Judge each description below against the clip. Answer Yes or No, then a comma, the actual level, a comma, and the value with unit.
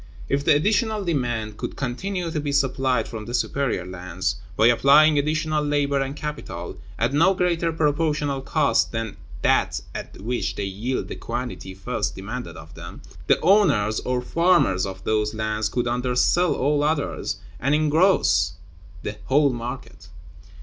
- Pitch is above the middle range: No, low, 135 Hz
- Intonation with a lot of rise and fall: Yes, wide, 5.9 semitones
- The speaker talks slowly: No, average, 150 wpm